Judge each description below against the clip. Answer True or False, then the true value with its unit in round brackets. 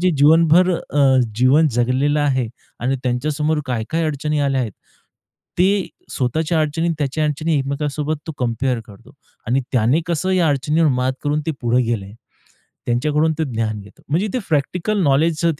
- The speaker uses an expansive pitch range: False (4.0 semitones)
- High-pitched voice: False (145 Hz)